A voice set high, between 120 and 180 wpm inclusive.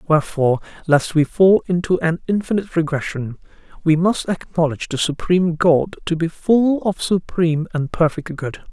No: medium, 170 Hz; average, 150 wpm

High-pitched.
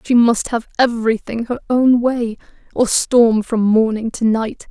Yes: high, 230 Hz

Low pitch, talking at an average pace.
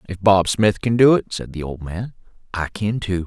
No: low, 100 Hz; fast, 240 wpm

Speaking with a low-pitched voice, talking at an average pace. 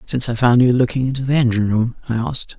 No: low, 120 Hz; fast, 255 wpm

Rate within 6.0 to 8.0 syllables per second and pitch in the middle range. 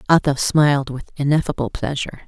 Yes: 6.1 syllables/s; medium, 145 Hz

